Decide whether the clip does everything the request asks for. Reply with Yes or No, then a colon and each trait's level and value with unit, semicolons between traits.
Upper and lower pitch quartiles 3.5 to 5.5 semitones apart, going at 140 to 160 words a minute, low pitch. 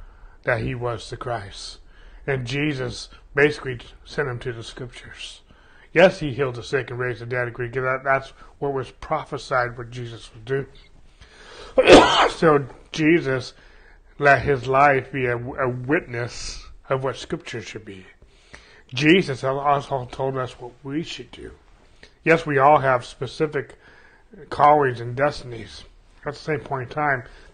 No: average, 2.9 semitones; average, 155 wpm; low, 130 Hz